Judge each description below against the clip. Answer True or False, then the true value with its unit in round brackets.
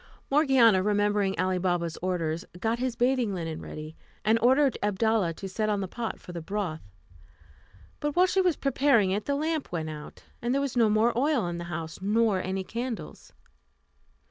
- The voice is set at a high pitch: True (210 Hz)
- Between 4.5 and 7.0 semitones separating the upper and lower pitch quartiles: True (5.4 semitones)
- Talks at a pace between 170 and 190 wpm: True (180 wpm)